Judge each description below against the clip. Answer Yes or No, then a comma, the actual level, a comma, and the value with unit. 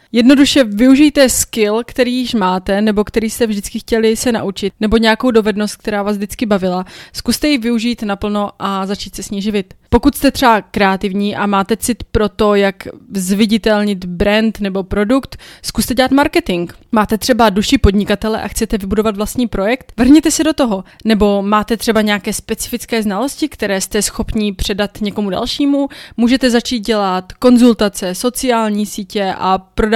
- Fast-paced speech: No, average, 160 wpm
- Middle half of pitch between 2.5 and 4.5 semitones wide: Yes, average, 2.8 semitones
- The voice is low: No, high, 220 Hz